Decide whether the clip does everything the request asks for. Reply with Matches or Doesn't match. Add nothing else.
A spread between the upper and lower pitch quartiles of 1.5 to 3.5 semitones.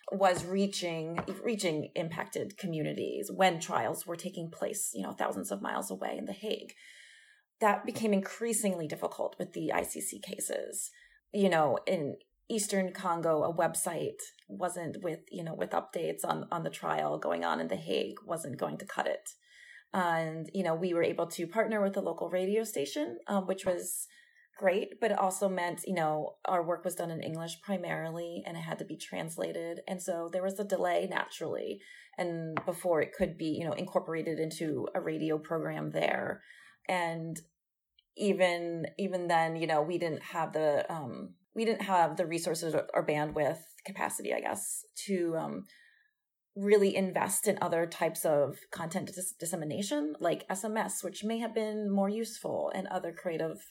Doesn't match